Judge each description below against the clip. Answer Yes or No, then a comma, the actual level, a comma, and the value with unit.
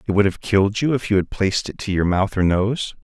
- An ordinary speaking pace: No, fast, 295 wpm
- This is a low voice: Yes, low, 100 Hz